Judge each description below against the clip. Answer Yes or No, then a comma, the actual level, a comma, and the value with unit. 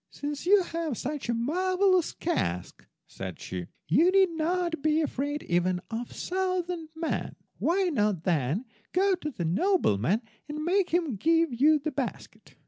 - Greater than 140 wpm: Yes, average, 155 wpm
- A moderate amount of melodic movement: No, wide, 7.9 semitones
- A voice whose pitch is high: Yes, very high, 310 Hz